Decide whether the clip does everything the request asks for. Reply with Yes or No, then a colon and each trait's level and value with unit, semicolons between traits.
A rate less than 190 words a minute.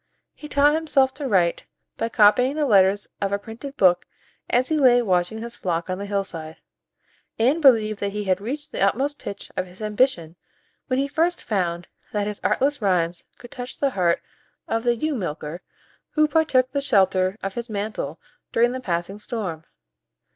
Yes: average, 180 wpm